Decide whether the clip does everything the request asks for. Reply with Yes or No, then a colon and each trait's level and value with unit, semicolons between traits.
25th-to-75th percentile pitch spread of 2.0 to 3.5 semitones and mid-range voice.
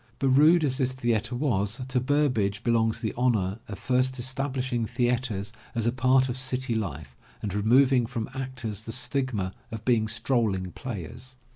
No: average, 3.1 semitones; low, 120 Hz